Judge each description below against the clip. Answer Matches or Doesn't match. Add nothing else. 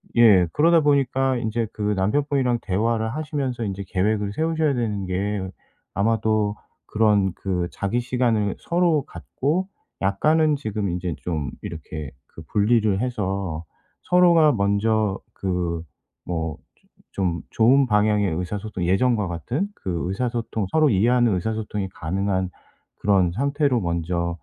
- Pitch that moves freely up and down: Doesn't match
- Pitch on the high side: Doesn't match